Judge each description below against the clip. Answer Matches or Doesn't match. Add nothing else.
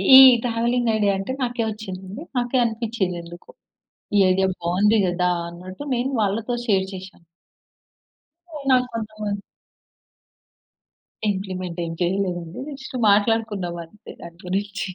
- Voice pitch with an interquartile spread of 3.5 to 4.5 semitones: Matches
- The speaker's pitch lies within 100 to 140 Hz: Doesn't match